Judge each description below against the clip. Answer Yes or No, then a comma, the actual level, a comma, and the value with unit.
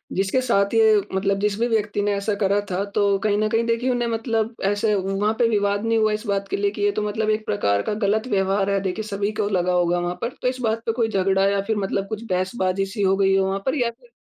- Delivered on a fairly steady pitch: Yes, narrow, 2.3 semitones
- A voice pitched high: Yes, high, 205 Hz